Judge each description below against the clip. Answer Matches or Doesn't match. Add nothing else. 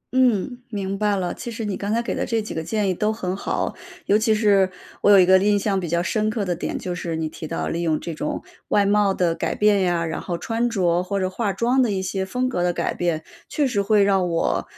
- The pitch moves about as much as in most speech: Matches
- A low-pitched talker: Doesn't match